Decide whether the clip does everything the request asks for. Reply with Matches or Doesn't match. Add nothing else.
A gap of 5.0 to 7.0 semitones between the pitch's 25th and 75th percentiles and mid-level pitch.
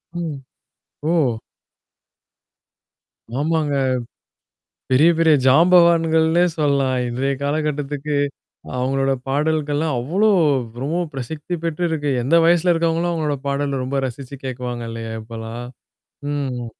Doesn't match